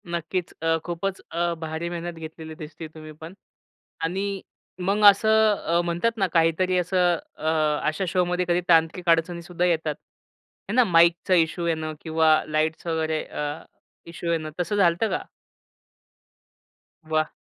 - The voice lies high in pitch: No, medium, 170 Hz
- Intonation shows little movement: Yes, narrow, 2.2 semitones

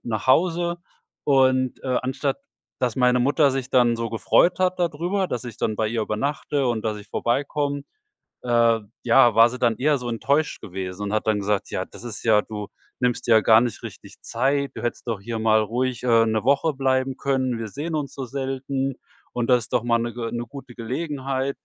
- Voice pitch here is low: Yes, low, 125 Hz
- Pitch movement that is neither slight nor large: Yes, average, 3.3 semitones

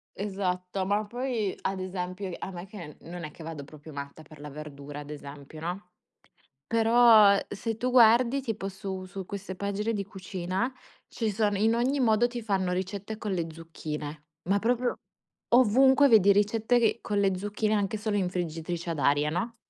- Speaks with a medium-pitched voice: No, high, 195 Hz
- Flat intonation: No, average, 4.2 semitones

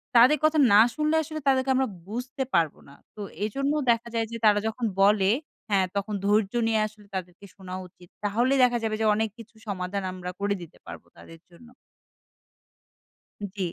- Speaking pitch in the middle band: No, high, 215 Hz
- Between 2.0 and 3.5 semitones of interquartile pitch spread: No, average, 4.0 semitones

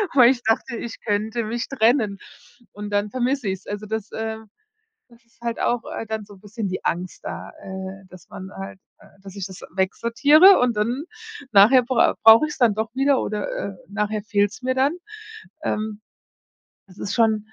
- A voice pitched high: Yes, high, 220 Hz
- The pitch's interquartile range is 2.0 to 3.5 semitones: Yes, average, 2.9 semitones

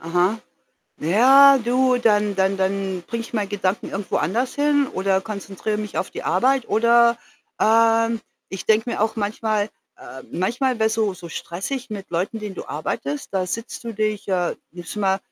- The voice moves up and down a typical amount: Yes, average, 3.5 semitones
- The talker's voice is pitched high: Yes, high, 215 Hz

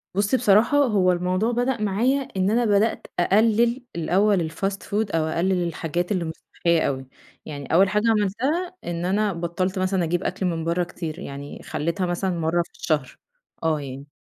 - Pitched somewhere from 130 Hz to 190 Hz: Yes, medium, 185 Hz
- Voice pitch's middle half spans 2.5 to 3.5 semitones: No, average, 4.0 semitones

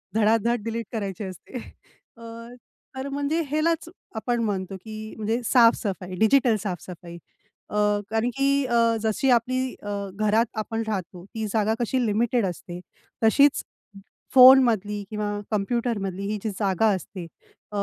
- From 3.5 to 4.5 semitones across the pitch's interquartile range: No, average, 3.0 semitones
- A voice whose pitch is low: No, high, 220 Hz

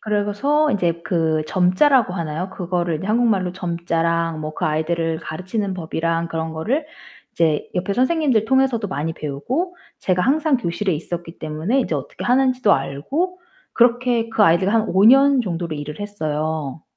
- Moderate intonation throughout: No, wide, 6.6 semitones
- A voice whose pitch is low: No, medium, 185 Hz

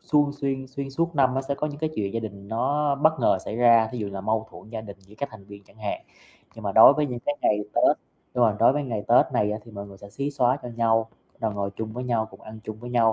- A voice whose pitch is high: No, low, 115 Hz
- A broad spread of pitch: No, average, 4.2 semitones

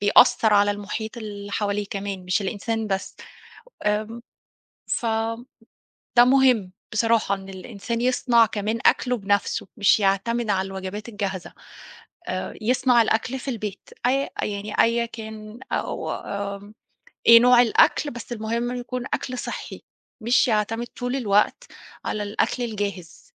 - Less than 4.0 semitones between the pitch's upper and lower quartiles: Yes, average, 2.8 semitones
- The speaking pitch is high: Yes, high, 220 Hz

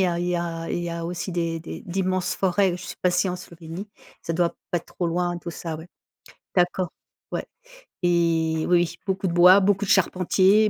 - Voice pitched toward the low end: No, medium, 175 Hz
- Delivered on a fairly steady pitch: Yes, narrow, 1.7 semitones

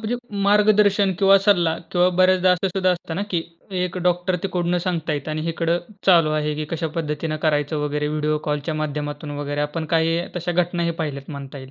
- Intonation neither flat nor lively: Yes, average, 3.2 semitones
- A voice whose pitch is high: No, medium, 165 Hz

